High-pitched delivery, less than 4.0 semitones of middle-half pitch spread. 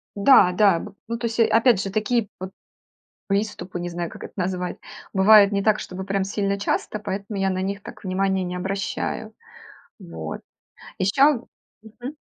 Yes: high, 200 Hz; narrow, 2.4 semitones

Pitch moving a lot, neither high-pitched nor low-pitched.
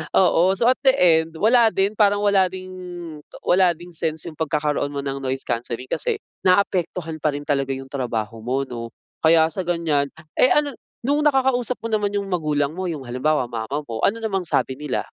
Yes: wide, 6.2 semitones; medium, 160 Hz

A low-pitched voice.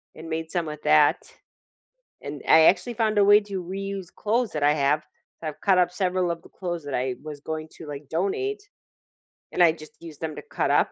No: medium, 165 Hz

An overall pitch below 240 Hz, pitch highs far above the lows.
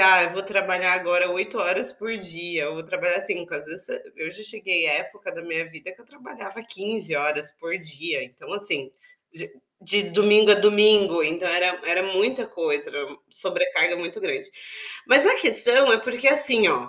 No: high, 190 Hz; average, 4.1 semitones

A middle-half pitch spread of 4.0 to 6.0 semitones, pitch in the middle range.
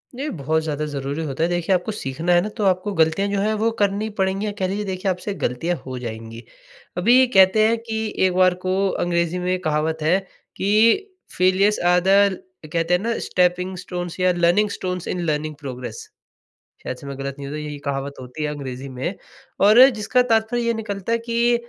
Yes: average, 5.2 semitones; medium, 180 Hz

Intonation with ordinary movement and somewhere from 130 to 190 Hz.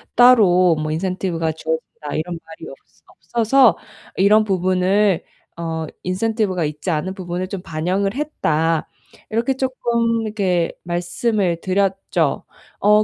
Yes: average, 4.3 semitones; medium, 185 Hz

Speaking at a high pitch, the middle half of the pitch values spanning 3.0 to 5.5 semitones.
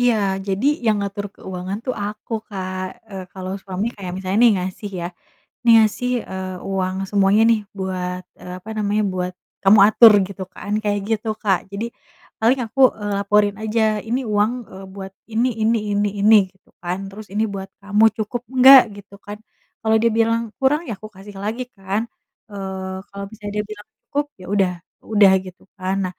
No: high, 205 Hz; narrow, 2.5 semitones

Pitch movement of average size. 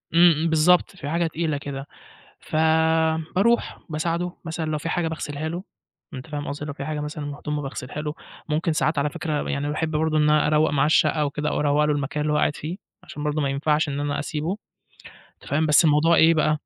No: narrow, 1.7 semitones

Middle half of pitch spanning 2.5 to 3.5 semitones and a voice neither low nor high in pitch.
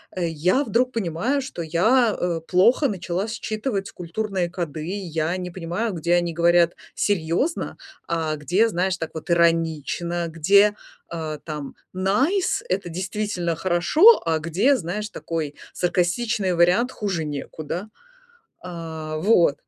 No: average, 4.0 semitones; medium, 175 Hz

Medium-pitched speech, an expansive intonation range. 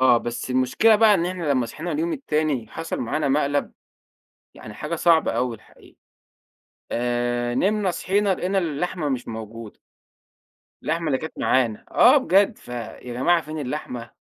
Yes: medium, 150 Hz; wide, 6.2 semitones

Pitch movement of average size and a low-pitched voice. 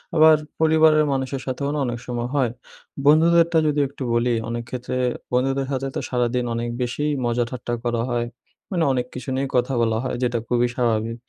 Yes: average, 3.0 semitones; low, 125 Hz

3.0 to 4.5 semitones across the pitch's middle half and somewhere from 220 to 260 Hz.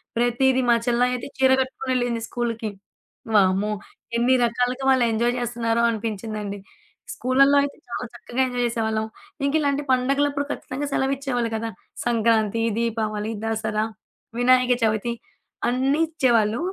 No: narrow, 2.6 semitones; high, 240 Hz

